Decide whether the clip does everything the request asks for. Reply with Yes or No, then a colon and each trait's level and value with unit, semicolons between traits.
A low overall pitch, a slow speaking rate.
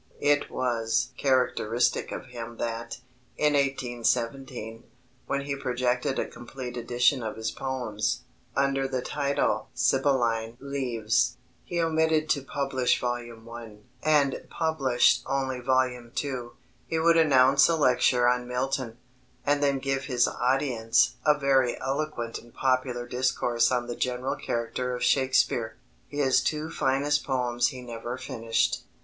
Yes: low, 130 Hz; slow, 130 wpm